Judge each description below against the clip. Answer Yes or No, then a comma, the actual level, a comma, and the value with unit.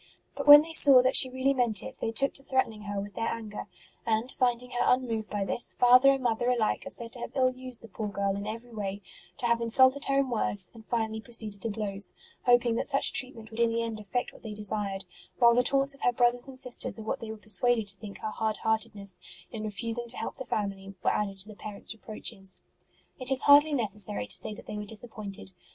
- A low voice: No, high, 230 Hz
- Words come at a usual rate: No, fast, 240 wpm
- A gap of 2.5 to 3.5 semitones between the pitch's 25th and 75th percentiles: Yes, average, 3.1 semitones